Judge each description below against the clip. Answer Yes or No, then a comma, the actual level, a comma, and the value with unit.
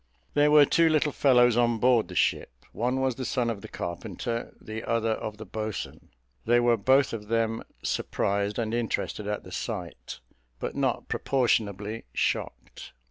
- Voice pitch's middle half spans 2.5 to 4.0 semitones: Yes, average, 2.8 semitones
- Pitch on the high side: No, low, 115 Hz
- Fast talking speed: No, average, 165 wpm